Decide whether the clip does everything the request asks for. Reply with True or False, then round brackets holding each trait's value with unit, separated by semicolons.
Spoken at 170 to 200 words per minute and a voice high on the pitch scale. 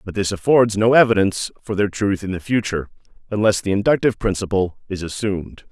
False (180 wpm; 100 Hz)